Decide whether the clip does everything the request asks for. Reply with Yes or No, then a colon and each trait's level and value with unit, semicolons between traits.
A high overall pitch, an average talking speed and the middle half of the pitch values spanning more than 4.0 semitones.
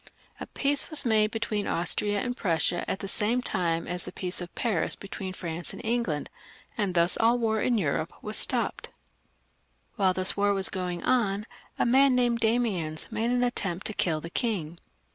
Yes: high, 205 Hz; average, 180 wpm; average, 4.8 semitones